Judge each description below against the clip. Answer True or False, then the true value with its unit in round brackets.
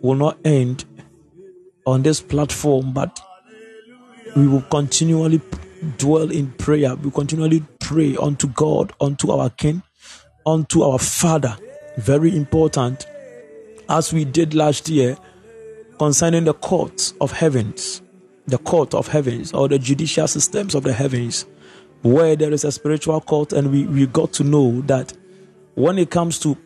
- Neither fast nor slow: True (145 wpm)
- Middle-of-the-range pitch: True (155 Hz)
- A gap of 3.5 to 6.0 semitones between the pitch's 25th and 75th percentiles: False (3.0 semitones)